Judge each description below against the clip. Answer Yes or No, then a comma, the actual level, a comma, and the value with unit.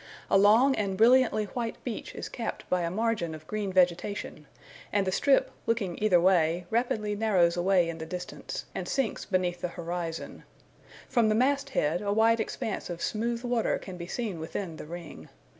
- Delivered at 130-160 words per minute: No, average, 180 wpm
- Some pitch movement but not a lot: Yes, average, 4.5 semitones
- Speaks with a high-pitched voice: Yes, high, 195 Hz